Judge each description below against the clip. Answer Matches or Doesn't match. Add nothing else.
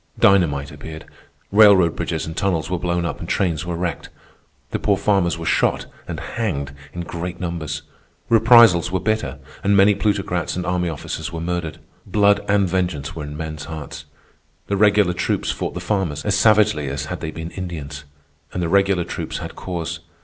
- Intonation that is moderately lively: Matches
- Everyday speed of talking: Matches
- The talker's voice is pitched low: Matches